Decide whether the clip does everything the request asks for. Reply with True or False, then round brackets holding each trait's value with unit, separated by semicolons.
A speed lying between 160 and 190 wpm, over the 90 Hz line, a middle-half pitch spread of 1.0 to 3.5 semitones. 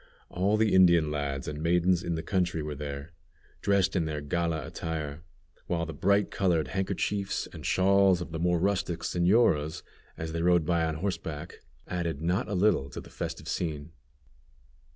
False (170 wpm; 85 Hz; 3.0 semitones)